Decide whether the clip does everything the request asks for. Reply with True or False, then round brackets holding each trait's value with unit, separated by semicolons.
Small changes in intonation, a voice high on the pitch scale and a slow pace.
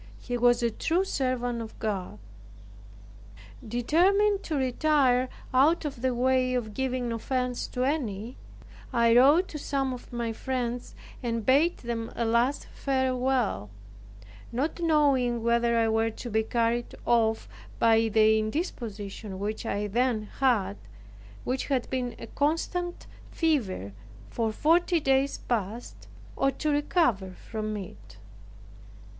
False (3.3 semitones; 245 Hz; 130 wpm)